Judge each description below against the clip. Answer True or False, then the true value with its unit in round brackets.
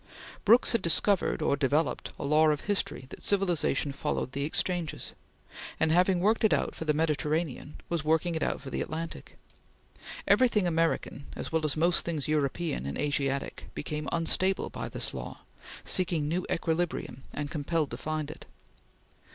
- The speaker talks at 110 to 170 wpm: True (160 wpm)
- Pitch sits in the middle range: True (160 Hz)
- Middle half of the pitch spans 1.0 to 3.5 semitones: True (3.0 semitones)